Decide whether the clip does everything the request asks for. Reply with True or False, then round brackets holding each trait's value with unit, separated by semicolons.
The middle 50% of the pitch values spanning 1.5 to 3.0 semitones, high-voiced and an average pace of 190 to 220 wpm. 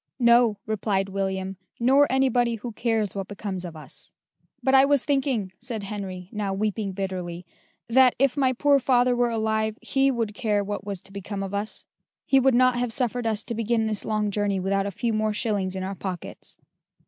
False (3.8 semitones; 215 Hz; 195 wpm)